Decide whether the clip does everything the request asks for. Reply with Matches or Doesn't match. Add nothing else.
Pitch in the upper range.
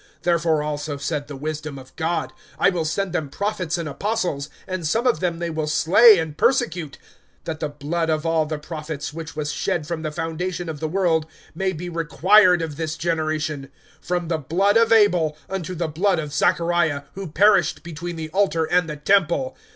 Doesn't match